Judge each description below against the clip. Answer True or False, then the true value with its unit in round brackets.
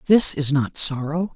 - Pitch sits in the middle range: True (155 Hz)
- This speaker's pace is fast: False (175 wpm)